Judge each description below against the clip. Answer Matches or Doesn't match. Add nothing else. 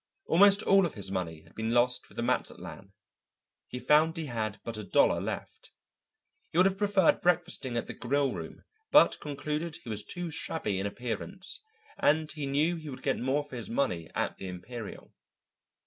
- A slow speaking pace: Doesn't match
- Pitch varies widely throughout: Matches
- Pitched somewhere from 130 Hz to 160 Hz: Matches